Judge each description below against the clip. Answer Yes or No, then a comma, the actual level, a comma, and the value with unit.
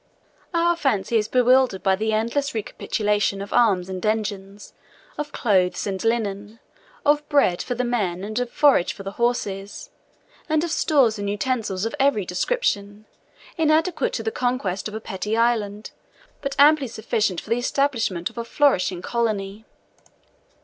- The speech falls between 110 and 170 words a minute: Yes, average, 150 wpm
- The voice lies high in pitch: Yes, high, 220 Hz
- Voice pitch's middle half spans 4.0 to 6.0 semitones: Yes, average, 4.8 semitones